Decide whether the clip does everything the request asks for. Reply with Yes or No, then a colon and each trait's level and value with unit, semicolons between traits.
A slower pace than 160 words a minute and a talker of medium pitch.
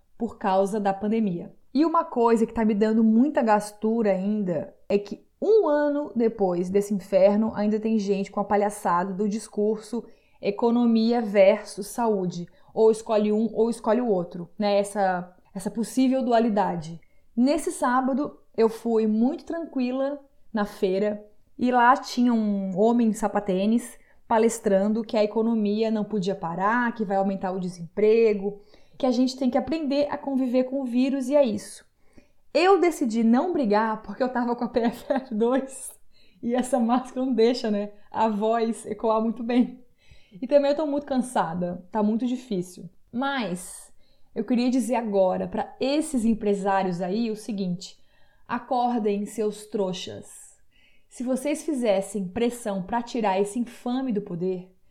No: average, 150 wpm; high, 220 Hz